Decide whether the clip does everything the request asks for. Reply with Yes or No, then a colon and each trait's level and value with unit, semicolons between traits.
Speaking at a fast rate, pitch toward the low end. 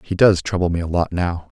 Yes: fast, 265 wpm; very low, 90 Hz